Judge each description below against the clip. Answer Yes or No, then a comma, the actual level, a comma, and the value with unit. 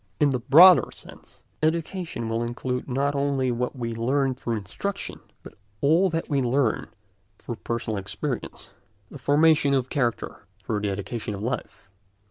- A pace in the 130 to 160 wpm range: Yes, average, 145 wpm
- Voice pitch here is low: Yes, low, 125 Hz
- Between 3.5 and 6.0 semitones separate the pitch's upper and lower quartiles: Yes, average, 3.9 semitones